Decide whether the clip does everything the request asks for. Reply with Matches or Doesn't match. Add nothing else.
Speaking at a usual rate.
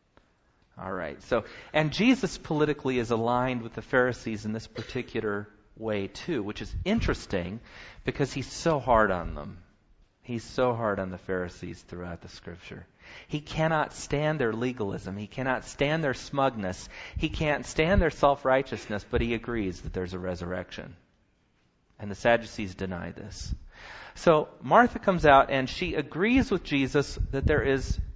Matches